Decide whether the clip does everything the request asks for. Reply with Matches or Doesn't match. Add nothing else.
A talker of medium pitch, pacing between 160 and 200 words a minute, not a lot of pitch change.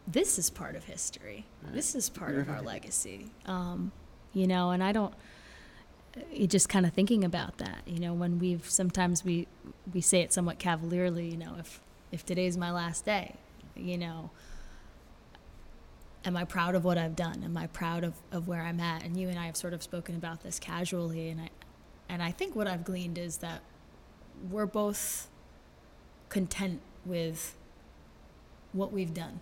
Matches